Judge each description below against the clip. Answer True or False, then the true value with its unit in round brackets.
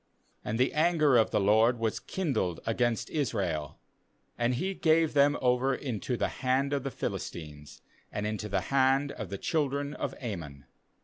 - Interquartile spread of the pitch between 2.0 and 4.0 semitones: False (5.2 semitones)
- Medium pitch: False (125 Hz)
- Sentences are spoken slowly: False (165 wpm)